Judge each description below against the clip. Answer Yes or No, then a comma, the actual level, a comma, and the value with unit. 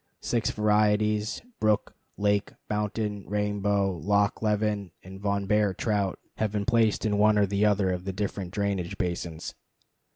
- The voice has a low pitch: Yes, low, 105 Hz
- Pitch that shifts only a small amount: Yes, narrow, 1.3 semitones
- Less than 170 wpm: Yes, average, 150 wpm